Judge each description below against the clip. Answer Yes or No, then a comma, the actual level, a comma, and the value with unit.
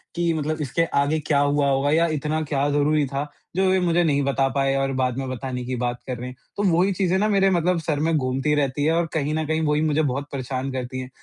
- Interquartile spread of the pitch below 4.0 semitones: Yes, average, 3.1 semitones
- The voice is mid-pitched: Yes, medium, 145 Hz